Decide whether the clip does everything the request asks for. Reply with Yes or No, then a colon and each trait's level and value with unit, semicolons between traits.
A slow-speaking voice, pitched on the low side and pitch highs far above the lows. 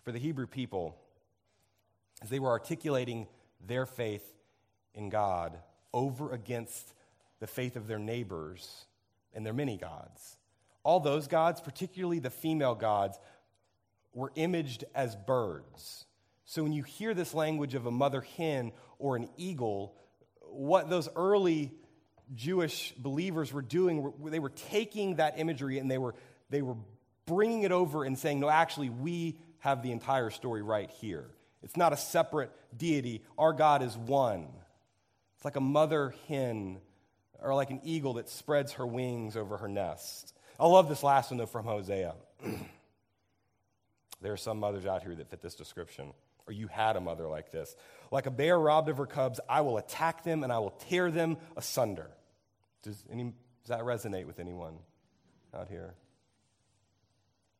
No: average, 160 wpm; low, 125 Hz; wide, 6.5 semitones